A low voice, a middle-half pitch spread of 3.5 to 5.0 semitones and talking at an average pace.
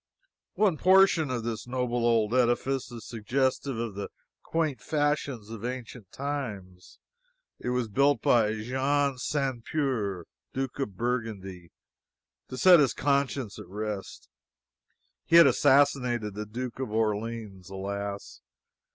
No: low, 120 Hz; average, 4.5 semitones; slow, 125 wpm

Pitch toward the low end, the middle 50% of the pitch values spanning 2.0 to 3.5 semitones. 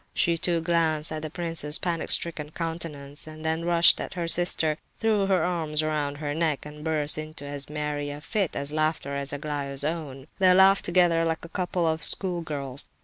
No: medium, 160 Hz; narrow, 2.4 semitones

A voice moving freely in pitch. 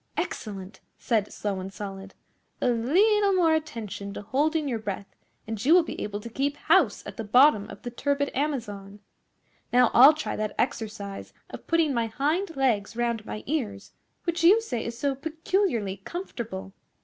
Yes: wide, 6.7 semitones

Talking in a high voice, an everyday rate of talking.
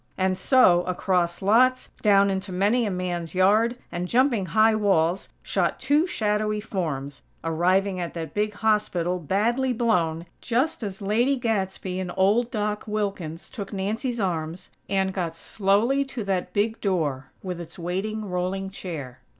Yes: high, 195 Hz; average, 150 wpm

